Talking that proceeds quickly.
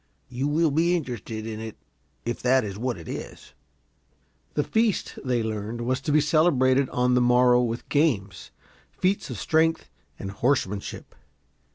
No: average, 155 wpm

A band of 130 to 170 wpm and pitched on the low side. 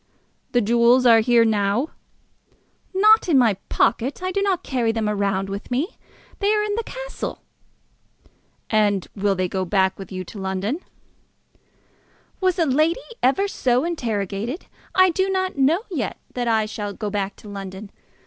No: average, 160 wpm; high, 235 Hz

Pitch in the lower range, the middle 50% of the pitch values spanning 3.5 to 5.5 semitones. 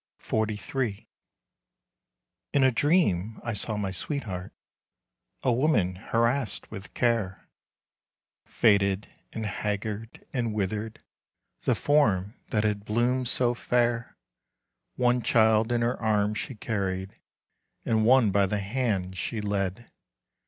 No: low, 110 Hz; average, 3.1 semitones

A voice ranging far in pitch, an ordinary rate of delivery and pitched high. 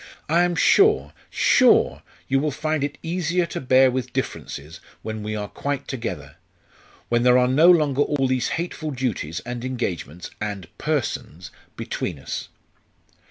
No: wide, 5.9 semitones; average, 150 wpm; low, 130 Hz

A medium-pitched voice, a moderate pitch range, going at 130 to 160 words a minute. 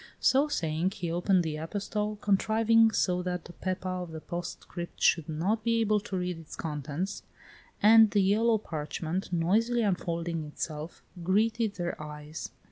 Yes: medium, 180 Hz; average, 4.3 semitones; average, 150 wpm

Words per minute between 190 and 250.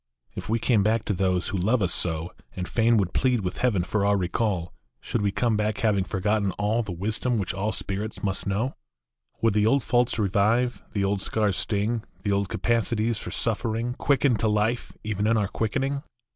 Yes: average, 200 wpm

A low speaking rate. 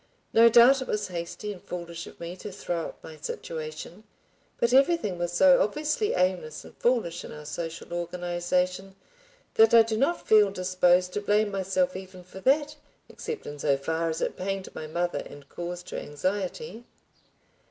No: average, 175 wpm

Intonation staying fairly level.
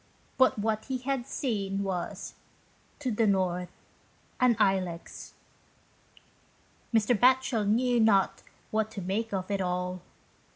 No: average, 4.0 semitones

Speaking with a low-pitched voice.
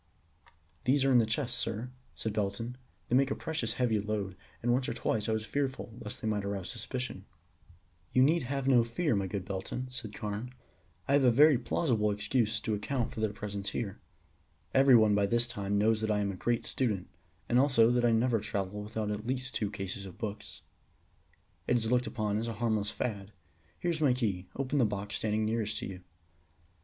Yes: low, 110 Hz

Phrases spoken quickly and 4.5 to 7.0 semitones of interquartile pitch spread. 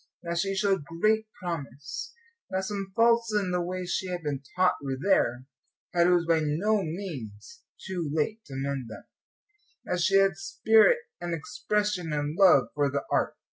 No: average, 175 wpm; average, 4.9 semitones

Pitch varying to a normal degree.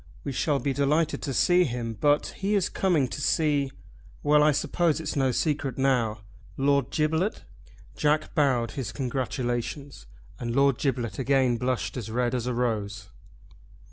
Yes: average, 3.4 semitones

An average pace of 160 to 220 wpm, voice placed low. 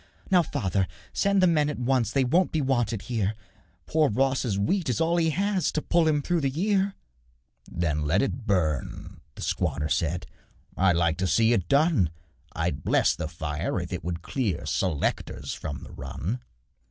Yes: average, 175 wpm; low, 120 Hz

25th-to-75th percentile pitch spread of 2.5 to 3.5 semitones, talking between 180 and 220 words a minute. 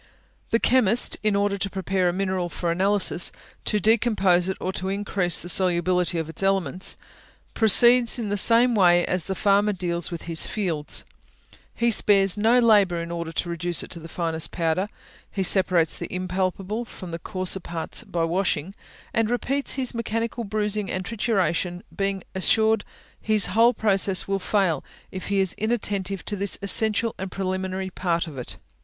No: average, 3.1 semitones; average, 170 wpm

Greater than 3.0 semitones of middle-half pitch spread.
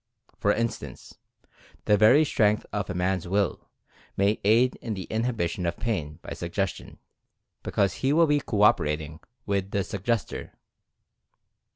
Yes: average, 3.7 semitones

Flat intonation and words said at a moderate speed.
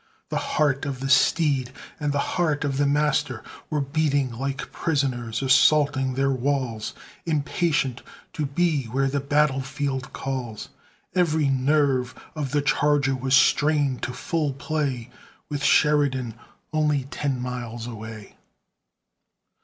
No: narrow, 2.3 semitones; slow, 130 wpm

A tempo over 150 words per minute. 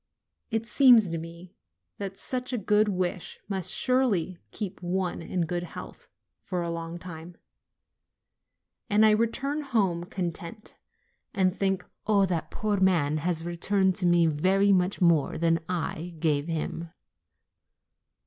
No: average, 140 wpm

